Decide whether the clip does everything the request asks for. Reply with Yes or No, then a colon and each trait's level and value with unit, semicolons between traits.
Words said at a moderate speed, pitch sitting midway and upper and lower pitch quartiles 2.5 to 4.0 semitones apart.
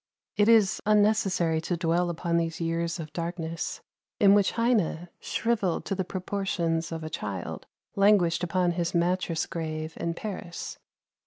Yes: average, 145 wpm; medium, 175 Hz; average, 3.0 semitones